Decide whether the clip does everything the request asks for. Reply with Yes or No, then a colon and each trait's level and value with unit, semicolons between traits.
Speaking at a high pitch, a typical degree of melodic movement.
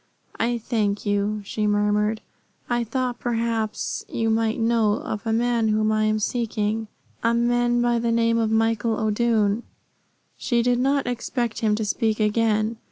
No: high, 225 Hz; narrow, 1.7 semitones